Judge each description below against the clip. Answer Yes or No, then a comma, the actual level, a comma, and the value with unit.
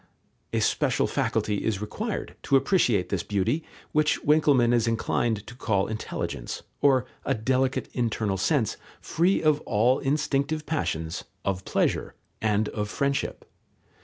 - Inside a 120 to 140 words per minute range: Yes, slow, 135 wpm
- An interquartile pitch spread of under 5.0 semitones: No, wide, 5.4 semitones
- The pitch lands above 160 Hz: No, low, 120 Hz